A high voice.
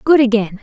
Yes: high, 240 Hz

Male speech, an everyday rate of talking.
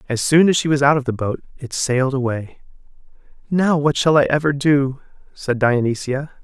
Yes: male; average, 185 wpm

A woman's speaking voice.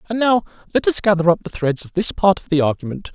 No: male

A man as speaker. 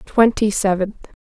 No: female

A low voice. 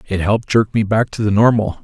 Yes: low, 105 Hz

